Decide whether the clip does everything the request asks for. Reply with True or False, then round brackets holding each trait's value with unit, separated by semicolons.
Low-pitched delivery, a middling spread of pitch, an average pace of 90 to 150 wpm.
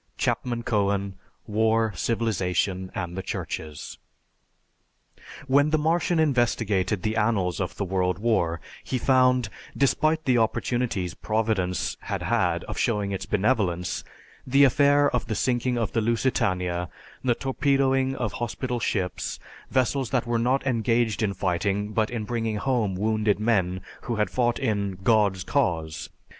True (110 Hz; 4.4 semitones; 140 wpm)